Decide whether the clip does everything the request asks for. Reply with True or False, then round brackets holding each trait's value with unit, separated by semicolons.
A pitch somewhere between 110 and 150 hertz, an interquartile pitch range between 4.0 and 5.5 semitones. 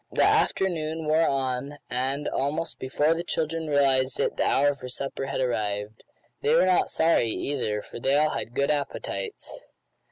False (140 Hz; 3.5 semitones)